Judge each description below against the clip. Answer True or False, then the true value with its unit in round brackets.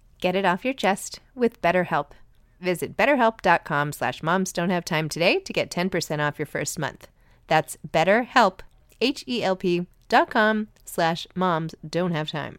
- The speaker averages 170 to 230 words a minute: False (145 wpm)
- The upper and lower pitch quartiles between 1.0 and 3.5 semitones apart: False (4.4 semitones)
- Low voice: False (175 Hz)